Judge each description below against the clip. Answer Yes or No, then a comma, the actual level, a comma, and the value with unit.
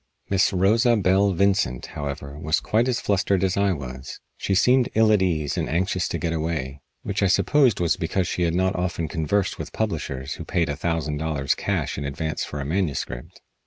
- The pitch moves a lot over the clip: No, average, 4.8 semitones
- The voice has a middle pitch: No, very low, 85 Hz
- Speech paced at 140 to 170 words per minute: No, average, 200 wpm